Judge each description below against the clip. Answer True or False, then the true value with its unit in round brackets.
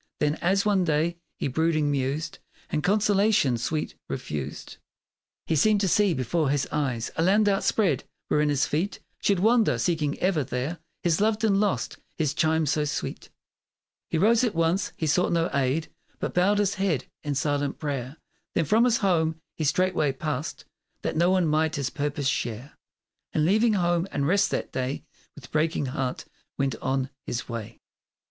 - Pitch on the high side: False (160 Hz)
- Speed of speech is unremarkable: True (170 wpm)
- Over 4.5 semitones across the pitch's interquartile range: True (5.0 semitones)